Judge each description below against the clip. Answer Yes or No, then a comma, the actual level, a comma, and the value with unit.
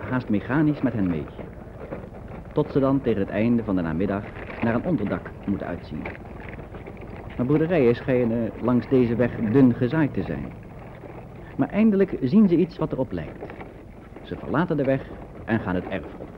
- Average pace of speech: Yes, average, 170 wpm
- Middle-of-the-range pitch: No, low, 120 Hz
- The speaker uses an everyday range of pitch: No, wide, 5.7 semitones